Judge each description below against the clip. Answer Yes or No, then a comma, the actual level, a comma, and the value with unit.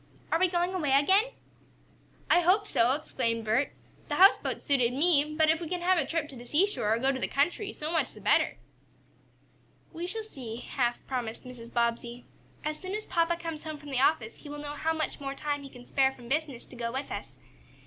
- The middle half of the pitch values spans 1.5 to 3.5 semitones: No, average, 5.2 semitones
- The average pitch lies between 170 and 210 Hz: No, very high, 290 Hz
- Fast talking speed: Yes, fast, 220 wpm